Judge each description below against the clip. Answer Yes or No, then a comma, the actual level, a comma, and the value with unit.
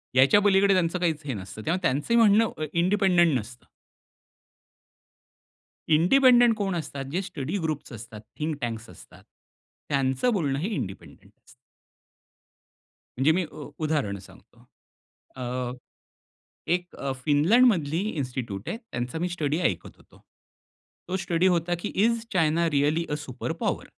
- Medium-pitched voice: Yes, medium, 160 Hz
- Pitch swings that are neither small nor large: No, wide, 5.7 semitones